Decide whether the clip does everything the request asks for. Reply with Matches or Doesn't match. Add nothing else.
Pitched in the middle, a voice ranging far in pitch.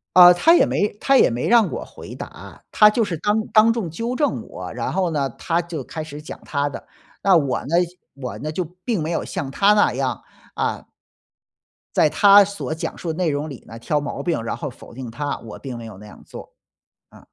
Matches